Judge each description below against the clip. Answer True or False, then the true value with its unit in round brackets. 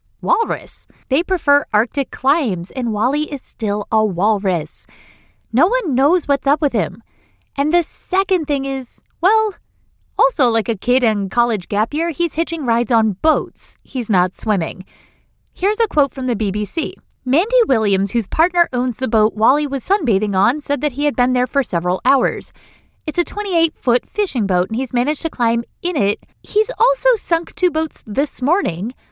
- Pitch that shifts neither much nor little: False (7.1 semitones)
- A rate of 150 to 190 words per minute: True (175 wpm)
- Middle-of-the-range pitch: False (265 Hz)